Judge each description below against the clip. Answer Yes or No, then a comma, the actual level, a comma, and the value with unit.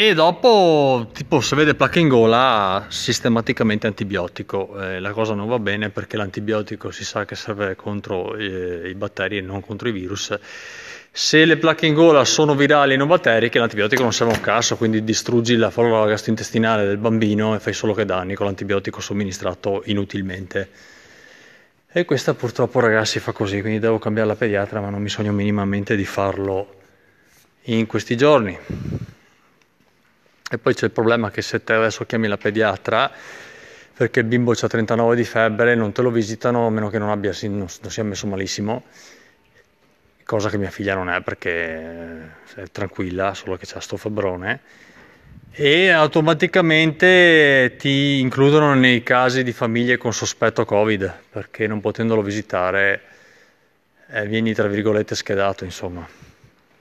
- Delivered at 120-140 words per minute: No, average, 160 wpm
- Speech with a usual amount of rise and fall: Yes, average, 3.3 semitones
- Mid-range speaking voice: No, low, 110 Hz